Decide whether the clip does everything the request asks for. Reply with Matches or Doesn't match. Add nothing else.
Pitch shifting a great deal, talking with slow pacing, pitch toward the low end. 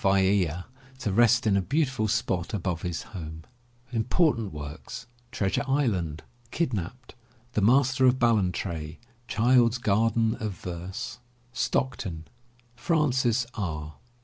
Matches